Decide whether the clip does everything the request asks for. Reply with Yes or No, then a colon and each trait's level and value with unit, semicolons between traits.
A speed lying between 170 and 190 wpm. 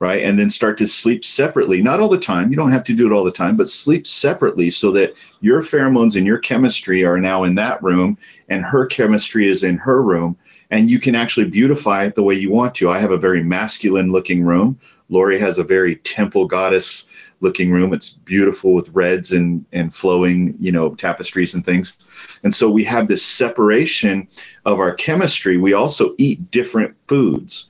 No: fast, 205 wpm